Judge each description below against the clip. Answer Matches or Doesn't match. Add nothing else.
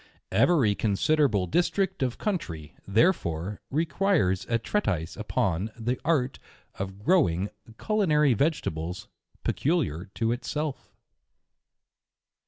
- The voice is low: Matches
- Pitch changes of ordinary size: Doesn't match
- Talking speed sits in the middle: Doesn't match